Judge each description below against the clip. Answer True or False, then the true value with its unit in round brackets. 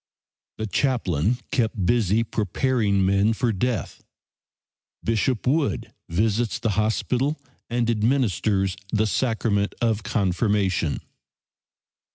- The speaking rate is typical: False (95 wpm)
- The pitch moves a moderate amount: True (3.2 semitones)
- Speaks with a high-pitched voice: False (110 Hz)